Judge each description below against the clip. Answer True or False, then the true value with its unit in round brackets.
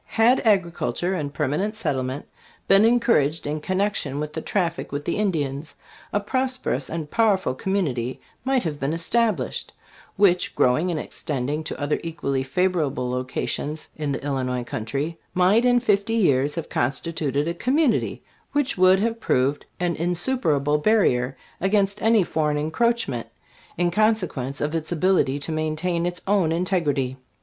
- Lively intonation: True (5.9 semitones)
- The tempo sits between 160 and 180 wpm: False (150 wpm)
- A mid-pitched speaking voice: True (165 Hz)